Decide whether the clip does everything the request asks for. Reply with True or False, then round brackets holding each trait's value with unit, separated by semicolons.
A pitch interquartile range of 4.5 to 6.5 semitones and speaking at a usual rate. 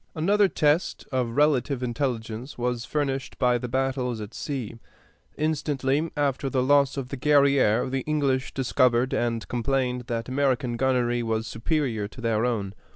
False (2.8 semitones; 150 wpm)